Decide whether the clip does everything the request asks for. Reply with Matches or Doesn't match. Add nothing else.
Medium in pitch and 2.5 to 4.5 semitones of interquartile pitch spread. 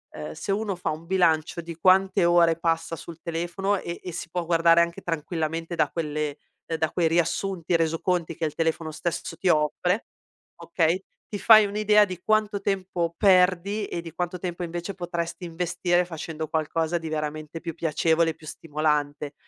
Doesn't match